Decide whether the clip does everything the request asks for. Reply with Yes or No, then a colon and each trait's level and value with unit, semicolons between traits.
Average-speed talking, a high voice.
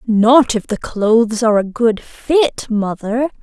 Yes: average, 160 wpm; high, 230 Hz